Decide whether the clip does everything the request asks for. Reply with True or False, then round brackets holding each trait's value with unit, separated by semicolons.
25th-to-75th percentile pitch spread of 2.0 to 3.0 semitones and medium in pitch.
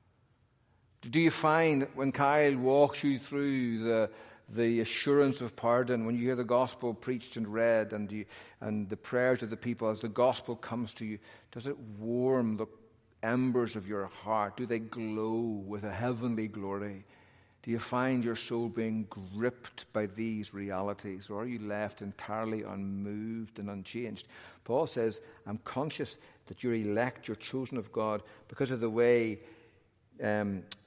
False (2.7 semitones; 115 Hz)